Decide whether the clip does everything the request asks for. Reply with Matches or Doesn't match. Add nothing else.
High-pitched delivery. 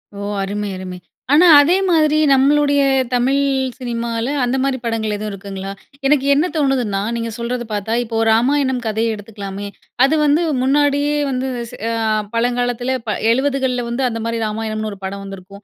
Matches